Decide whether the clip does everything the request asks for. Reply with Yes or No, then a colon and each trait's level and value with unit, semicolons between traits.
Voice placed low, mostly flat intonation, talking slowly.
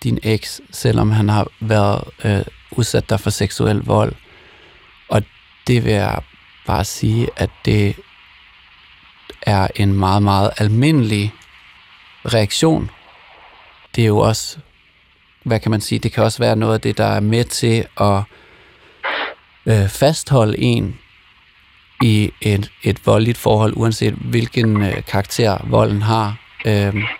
Yes: low, 110 Hz; narrow, 2.1 semitones; slow, 135 wpm